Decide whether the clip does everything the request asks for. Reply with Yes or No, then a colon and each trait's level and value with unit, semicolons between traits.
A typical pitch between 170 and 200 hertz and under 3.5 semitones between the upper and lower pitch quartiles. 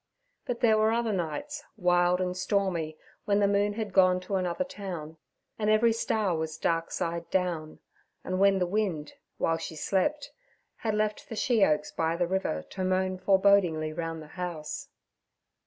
No: medium, 185 Hz; average, 3.8 semitones